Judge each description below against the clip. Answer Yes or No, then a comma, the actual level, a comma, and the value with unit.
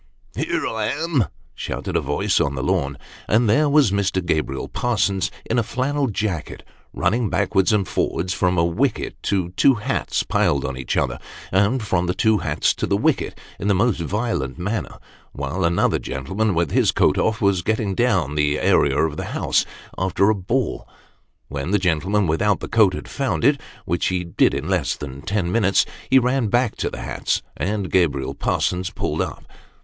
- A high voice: No, very low, 95 Hz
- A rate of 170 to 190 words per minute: Yes, average, 185 wpm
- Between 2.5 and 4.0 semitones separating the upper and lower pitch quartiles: No, average, 4.7 semitones